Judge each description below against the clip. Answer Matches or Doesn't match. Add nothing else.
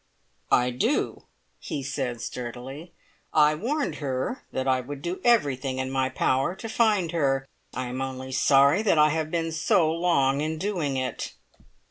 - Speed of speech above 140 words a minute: Matches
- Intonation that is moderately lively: Matches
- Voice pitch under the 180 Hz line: Matches